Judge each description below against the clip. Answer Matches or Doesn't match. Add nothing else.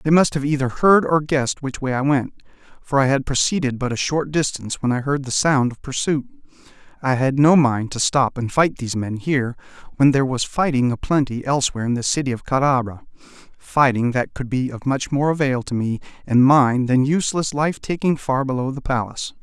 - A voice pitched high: Doesn't match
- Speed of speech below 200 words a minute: Doesn't match